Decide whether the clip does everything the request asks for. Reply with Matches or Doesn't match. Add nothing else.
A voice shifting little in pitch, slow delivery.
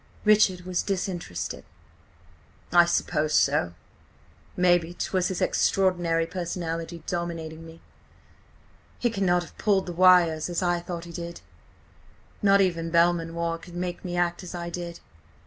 Matches